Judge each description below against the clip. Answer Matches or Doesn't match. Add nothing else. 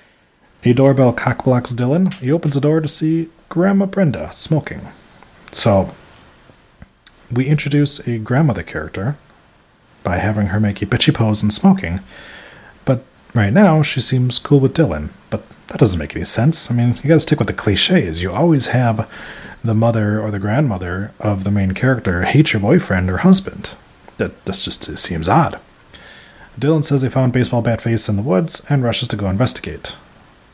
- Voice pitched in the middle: Doesn't match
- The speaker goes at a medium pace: Matches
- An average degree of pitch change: Doesn't match